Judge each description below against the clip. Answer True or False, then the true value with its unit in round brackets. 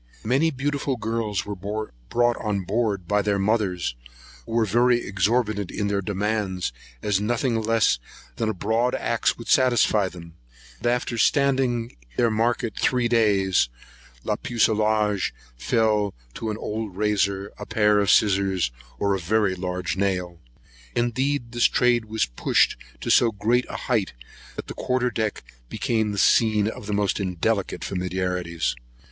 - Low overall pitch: True (105 Hz)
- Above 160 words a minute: False (155 wpm)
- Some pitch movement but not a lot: True (3.3 semitones)